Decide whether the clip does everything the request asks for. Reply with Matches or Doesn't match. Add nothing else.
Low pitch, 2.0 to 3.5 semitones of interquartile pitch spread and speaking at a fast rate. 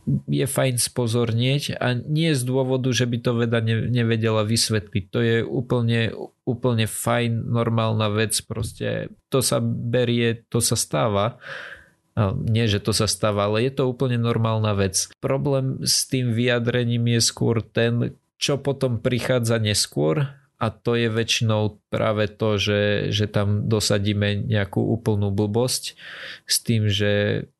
Doesn't match